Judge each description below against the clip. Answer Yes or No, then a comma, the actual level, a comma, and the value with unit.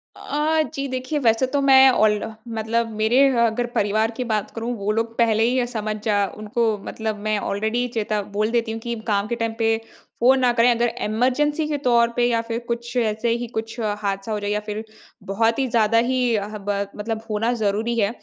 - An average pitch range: No, narrow, 2.2 semitones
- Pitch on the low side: No, high, 230 Hz